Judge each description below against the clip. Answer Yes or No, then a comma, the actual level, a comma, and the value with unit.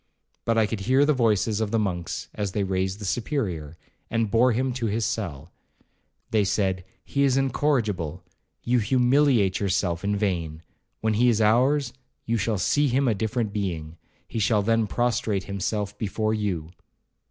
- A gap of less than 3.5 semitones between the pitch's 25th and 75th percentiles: No, average, 3.9 semitones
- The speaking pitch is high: No, low, 110 Hz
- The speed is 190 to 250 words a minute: No, average, 155 wpm